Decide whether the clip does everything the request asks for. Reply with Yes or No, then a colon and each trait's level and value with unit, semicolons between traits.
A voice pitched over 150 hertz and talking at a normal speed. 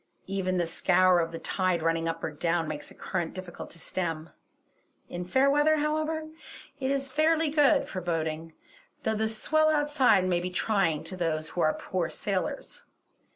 Yes: medium, 185 Hz; average, 175 wpm